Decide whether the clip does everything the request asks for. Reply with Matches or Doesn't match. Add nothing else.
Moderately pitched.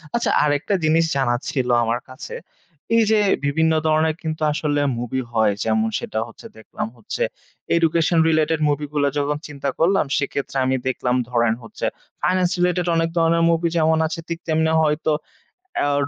Matches